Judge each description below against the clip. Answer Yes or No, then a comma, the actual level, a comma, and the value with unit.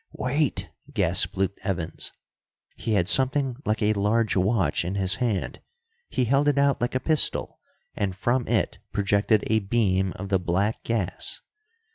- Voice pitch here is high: No, low, 105 Hz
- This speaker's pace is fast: No, average, 155 wpm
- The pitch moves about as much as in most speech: Yes, average, 4.2 semitones